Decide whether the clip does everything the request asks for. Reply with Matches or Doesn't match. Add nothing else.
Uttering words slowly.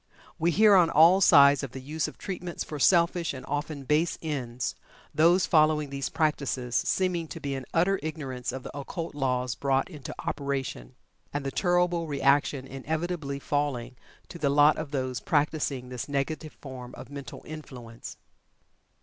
Doesn't match